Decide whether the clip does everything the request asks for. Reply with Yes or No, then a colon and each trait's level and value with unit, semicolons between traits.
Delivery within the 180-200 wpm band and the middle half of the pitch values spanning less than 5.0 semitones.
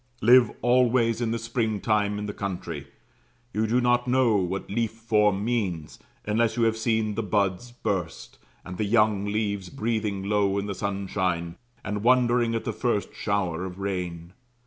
No: average, 165 wpm; average, 3.0 semitones